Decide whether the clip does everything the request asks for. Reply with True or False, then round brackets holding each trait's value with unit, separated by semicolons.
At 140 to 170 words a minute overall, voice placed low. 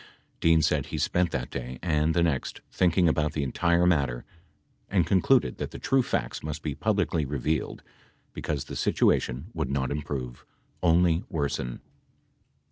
True (160 wpm; 75 Hz)